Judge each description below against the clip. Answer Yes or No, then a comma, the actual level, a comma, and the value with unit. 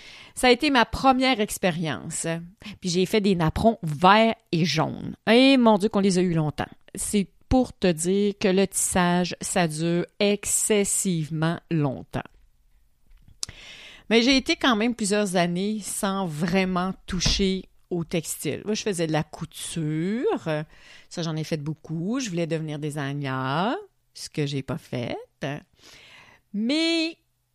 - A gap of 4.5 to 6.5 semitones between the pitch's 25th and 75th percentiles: Yes, average, 4.9 semitones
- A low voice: No, medium, 185 Hz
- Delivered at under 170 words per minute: Yes, slow, 145 wpm